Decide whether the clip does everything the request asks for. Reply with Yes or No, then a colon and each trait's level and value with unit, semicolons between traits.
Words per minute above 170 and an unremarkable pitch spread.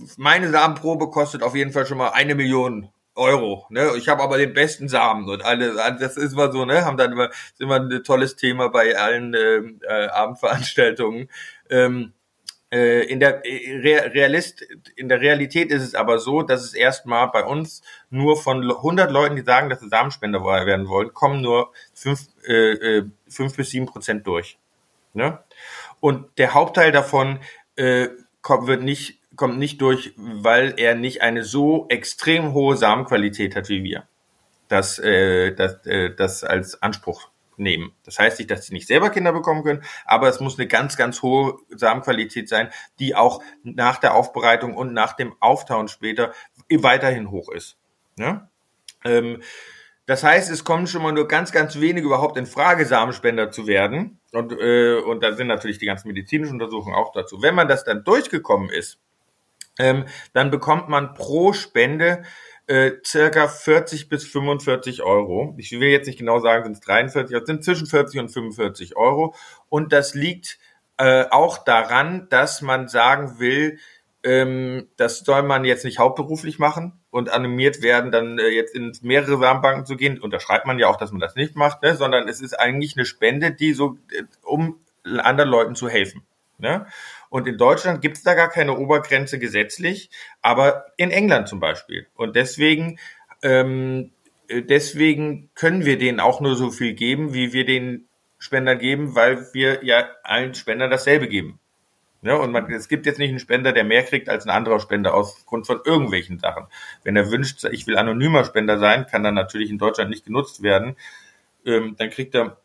Yes: average, 180 wpm; average, 3.6 semitones